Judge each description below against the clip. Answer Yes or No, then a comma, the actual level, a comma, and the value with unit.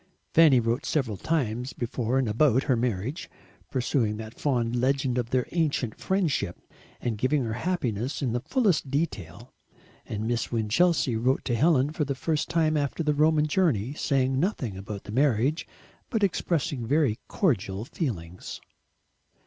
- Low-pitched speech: Yes, low, 130 Hz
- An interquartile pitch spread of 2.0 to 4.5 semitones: No, average, 4.9 semitones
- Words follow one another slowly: No, average, 150 wpm